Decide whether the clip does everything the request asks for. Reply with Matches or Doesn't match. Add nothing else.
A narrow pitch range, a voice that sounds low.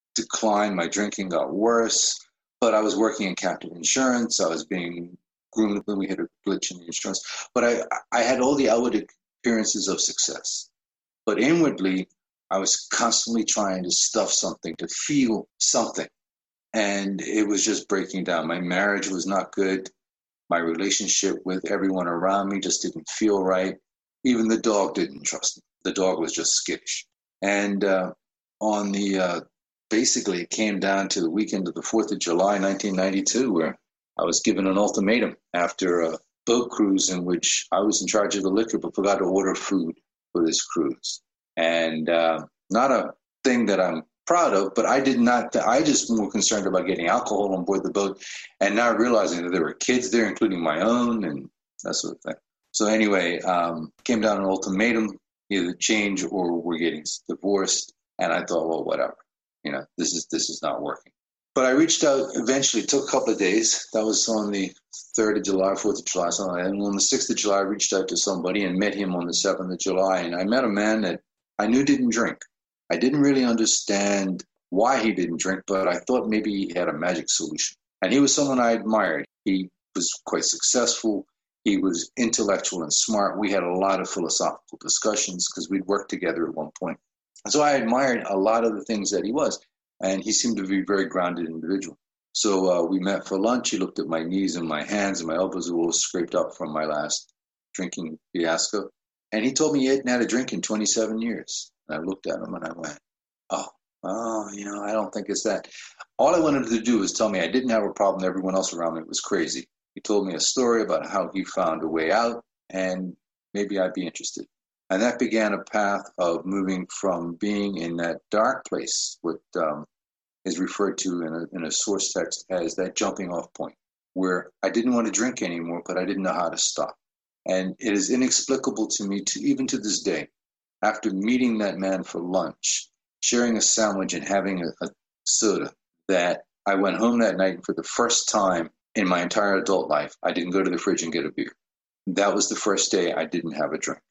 Doesn't match